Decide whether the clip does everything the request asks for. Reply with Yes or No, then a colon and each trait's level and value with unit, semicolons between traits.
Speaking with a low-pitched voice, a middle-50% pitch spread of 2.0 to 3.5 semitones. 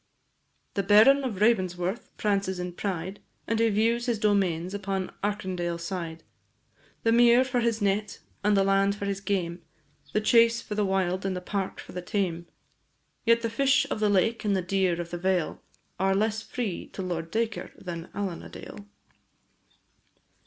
No: high, 200 Hz; average, 3.2 semitones